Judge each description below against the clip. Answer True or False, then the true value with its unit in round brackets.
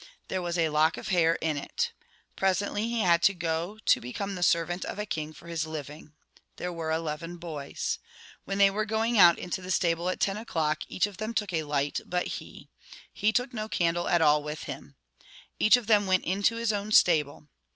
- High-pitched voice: False (175 Hz)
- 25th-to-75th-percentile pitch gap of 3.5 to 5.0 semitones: True (4.2 semitones)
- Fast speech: True (210 wpm)